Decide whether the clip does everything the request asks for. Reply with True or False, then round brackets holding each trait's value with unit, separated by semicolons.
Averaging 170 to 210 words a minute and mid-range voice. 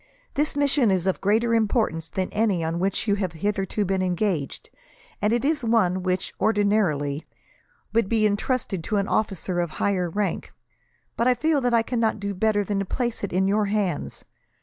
False (175 wpm; 205 Hz)